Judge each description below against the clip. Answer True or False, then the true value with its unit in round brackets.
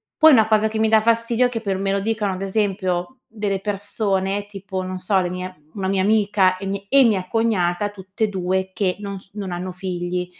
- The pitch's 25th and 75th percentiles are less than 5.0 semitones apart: True (2.6 semitones)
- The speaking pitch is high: True (195 Hz)